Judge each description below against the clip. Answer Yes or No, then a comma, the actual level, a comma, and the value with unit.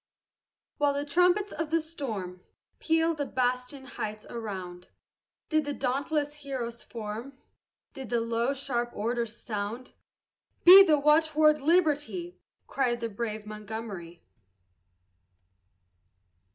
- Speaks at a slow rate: Yes, slow, 110 wpm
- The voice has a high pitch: Yes, very high, 260 Hz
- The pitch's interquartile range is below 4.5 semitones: No, average, 5.1 semitones